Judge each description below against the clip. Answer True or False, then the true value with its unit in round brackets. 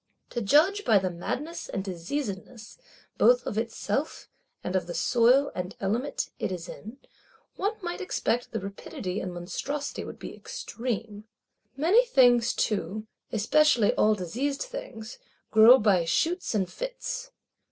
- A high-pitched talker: True (230 Hz)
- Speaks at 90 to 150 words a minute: True (140 wpm)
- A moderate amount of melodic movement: False (6.9 semitones)